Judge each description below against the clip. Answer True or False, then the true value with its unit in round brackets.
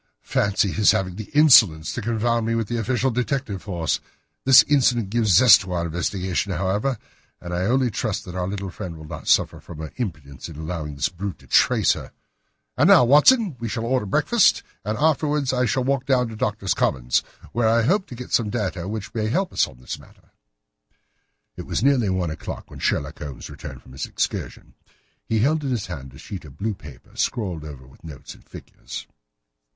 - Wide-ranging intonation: True (6.0 semitones)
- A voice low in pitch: True (105 Hz)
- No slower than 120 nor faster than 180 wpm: False (200 wpm)